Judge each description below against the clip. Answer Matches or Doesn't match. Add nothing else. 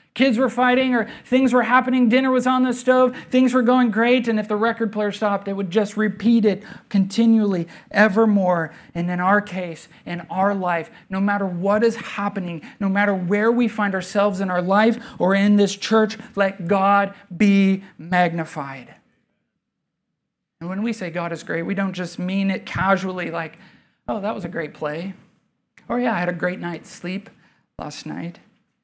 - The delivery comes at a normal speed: Matches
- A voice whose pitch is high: Matches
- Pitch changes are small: Doesn't match